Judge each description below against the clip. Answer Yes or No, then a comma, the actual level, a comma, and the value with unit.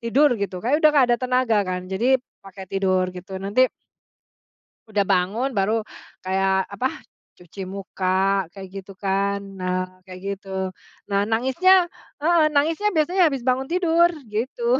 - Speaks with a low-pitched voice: No, high, 200 Hz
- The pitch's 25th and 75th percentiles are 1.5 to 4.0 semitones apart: No, wide, 5.6 semitones